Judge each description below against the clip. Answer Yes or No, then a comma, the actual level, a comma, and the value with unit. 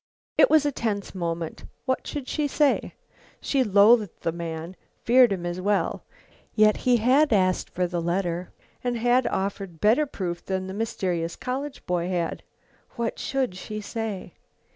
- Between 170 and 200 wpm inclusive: No, average, 160 wpm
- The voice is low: No, high, 205 Hz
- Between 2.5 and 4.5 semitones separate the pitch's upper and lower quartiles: No, wide, 5.6 semitones